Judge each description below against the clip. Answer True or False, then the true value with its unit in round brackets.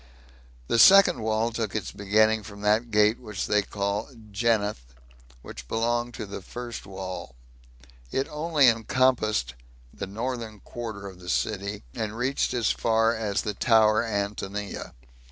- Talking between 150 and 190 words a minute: False (140 wpm)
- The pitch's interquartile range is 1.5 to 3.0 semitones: True (2.5 semitones)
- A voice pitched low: True (110 Hz)